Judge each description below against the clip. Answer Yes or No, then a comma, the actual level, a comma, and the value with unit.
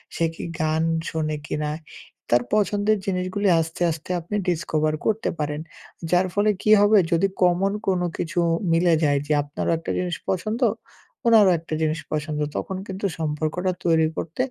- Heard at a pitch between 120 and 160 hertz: No, medium, 170 Hz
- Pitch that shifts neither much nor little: Yes, average, 3.7 semitones